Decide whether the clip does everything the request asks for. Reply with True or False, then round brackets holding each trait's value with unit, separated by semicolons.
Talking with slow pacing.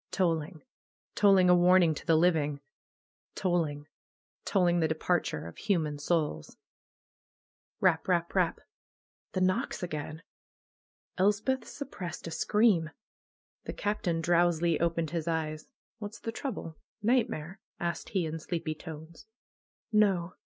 True (120 wpm)